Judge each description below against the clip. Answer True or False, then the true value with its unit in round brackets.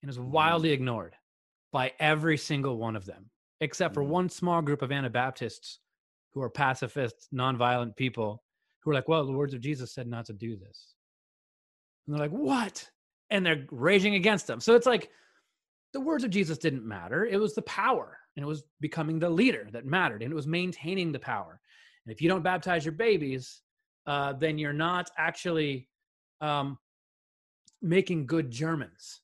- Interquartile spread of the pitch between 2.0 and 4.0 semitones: False (5.4 semitones)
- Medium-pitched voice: True (155 Hz)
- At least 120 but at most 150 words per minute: False (180 wpm)